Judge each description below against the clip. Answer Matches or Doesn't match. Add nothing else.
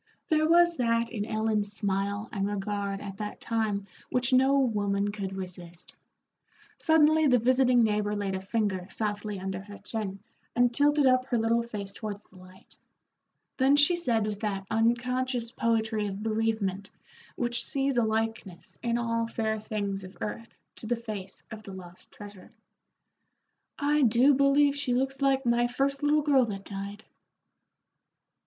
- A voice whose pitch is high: Matches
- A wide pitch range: Doesn't match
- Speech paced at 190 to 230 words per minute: Doesn't match